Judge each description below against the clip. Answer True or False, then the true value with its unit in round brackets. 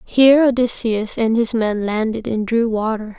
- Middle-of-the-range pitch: False (225 Hz)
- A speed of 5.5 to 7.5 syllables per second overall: False (4.6 syllables/s)